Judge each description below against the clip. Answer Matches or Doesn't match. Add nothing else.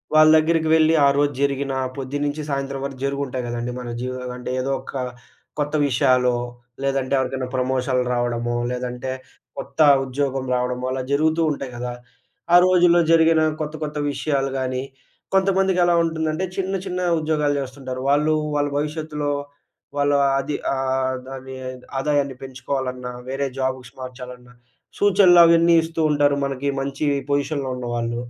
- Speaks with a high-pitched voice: Doesn't match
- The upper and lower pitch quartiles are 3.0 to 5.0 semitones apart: Matches